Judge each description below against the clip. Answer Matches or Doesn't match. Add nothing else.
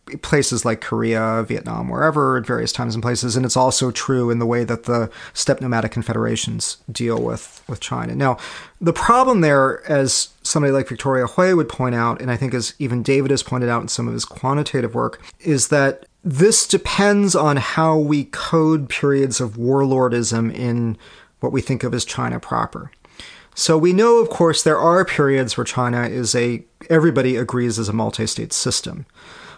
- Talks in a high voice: Doesn't match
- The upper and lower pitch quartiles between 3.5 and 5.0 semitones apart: Matches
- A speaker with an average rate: Matches